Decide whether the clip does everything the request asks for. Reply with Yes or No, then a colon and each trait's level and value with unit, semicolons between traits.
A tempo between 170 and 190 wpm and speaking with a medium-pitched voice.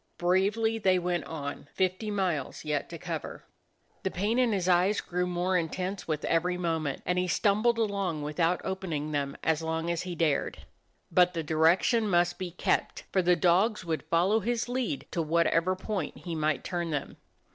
Yes: average, 180 wpm; medium, 180 Hz